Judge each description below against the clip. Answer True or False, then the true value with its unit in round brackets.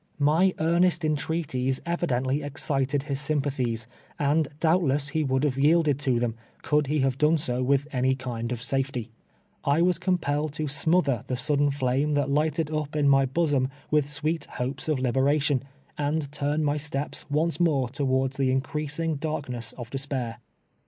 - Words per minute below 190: True (160 wpm)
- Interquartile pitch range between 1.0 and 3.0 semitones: True (2.6 semitones)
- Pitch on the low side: False (145 Hz)